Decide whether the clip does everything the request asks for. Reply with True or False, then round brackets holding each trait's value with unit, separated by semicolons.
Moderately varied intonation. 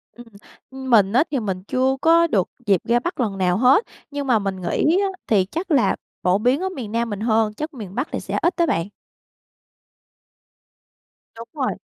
False (5.9 semitones)